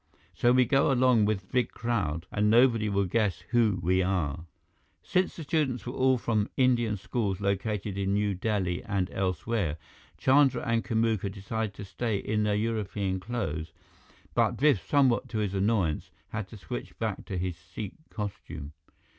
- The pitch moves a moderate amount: Yes, average, 3.7 semitones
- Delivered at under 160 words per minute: No, average, 165 wpm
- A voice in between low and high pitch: No, low, 105 Hz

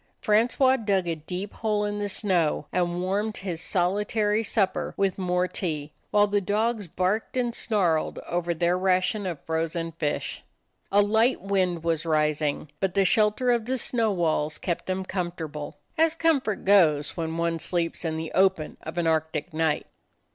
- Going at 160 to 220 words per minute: Yes, average, 165 wpm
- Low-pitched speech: No, medium, 185 Hz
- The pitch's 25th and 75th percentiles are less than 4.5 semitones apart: Yes, average, 4.0 semitones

